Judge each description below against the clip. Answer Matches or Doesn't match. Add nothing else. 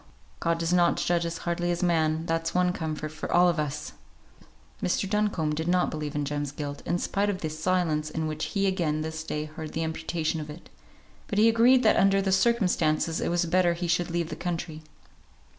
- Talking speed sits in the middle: Doesn't match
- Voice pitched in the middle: Matches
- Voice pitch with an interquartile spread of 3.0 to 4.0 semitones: Doesn't match